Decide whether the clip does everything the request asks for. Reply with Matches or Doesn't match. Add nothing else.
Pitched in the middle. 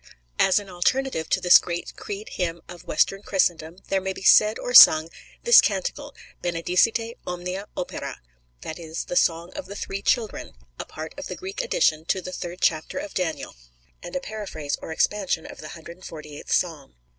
Matches